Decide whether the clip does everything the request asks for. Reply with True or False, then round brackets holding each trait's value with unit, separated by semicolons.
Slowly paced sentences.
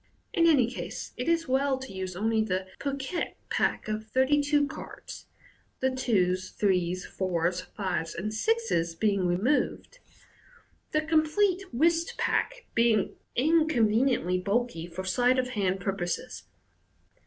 True (130 wpm)